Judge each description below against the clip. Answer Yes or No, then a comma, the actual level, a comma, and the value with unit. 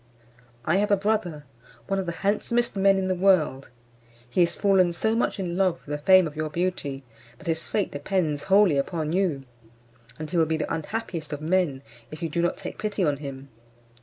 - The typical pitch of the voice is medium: Yes, medium, 175 Hz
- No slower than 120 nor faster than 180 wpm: No, fast, 205 wpm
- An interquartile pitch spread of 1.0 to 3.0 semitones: No, average, 4.2 semitones